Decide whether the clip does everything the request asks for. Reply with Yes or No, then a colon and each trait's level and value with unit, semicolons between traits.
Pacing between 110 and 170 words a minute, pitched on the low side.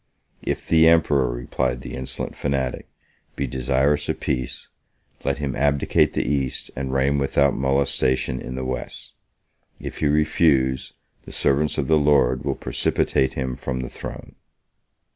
Yes: average, 145 wpm; very low, 65 Hz